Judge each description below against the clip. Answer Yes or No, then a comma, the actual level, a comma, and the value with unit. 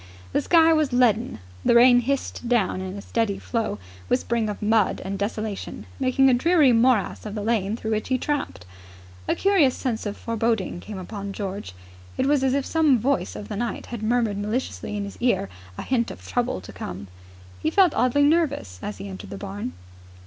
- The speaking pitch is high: Yes, high, 230 Hz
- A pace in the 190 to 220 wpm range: Yes, average, 195 wpm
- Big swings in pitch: No, average, 4.5 semitones